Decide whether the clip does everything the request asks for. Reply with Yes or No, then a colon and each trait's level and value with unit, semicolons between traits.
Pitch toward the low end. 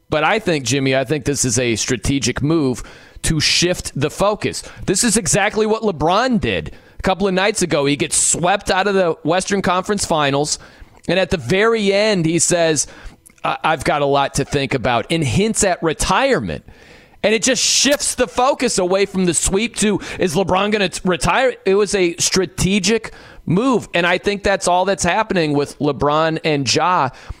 No: medium, 180 Hz